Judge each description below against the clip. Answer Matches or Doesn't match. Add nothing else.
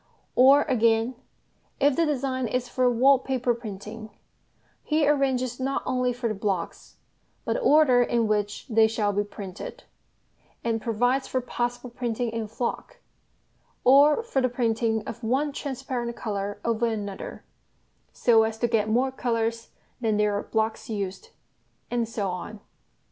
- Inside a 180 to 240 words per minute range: Doesn't match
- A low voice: Doesn't match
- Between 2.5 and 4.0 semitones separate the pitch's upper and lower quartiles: Matches